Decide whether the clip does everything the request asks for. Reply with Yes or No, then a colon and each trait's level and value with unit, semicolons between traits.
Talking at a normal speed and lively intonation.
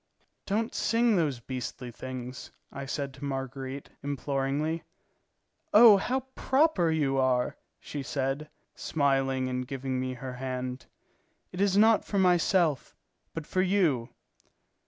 No: slow, 125 wpm; wide, 5.7 semitones